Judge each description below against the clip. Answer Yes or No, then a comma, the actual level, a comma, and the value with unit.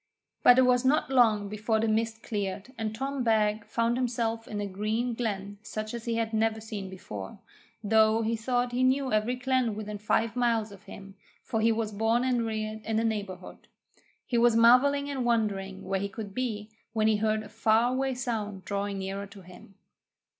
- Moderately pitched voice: No, high, 220 Hz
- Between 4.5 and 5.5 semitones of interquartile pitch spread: No, narrow, 2.5 semitones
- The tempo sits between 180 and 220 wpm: Yes, average, 195 wpm